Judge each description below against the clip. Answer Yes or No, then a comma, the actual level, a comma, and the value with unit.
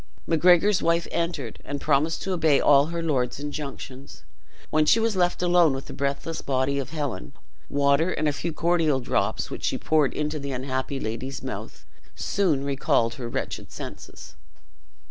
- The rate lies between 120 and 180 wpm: Yes, average, 165 wpm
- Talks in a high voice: No, medium, 145 Hz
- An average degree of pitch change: Yes, average, 3.6 semitones